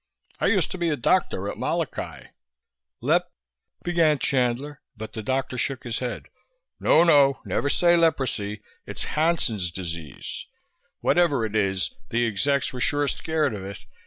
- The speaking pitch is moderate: No, low, 130 Hz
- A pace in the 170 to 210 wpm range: No, average, 155 wpm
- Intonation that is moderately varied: No, wide, 6.1 semitones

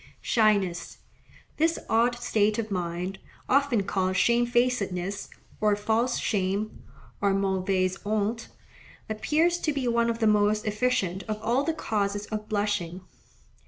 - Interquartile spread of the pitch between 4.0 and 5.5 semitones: No, average, 3.3 semitones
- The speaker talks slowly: Yes, slow, 125 wpm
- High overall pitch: Yes, high, 210 Hz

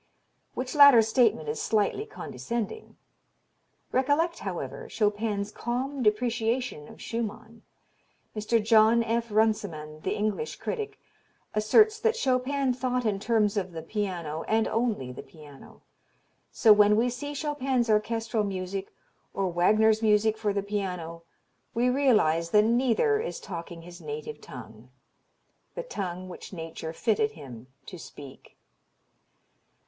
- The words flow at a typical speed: No, slow, 125 wpm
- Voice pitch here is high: Yes, high, 220 Hz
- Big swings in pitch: No, average, 4.6 semitones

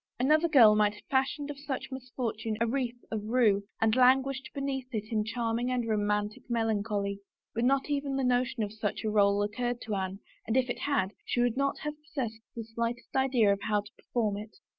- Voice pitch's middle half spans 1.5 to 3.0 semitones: No, average, 3.8 semitones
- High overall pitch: Yes, high, 235 Hz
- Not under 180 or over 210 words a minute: Yes, fast, 205 wpm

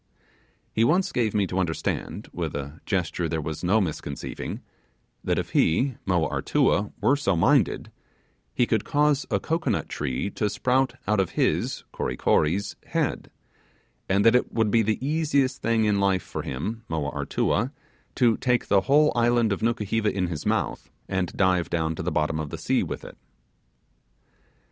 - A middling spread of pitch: No, wide, 5.7 semitones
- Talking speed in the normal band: Yes, average, 170 wpm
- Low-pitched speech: Yes, low, 100 Hz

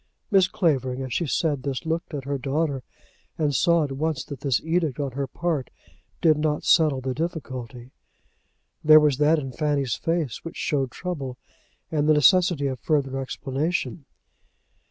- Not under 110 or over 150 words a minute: No, average, 160 wpm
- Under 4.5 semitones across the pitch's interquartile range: Yes, average, 3.2 semitones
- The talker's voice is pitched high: No, medium, 145 Hz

